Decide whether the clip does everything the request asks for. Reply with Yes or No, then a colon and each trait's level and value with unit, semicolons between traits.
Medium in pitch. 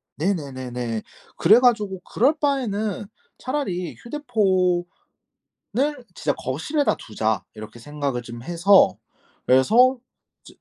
Yes: medium, 180 Hz